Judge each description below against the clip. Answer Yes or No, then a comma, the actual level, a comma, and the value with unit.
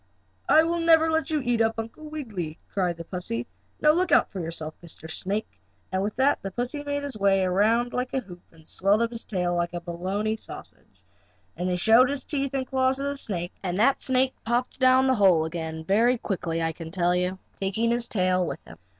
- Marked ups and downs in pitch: Yes, wide, 6.5 semitones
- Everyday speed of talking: No, fast, 220 wpm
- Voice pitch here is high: Yes, high, 215 Hz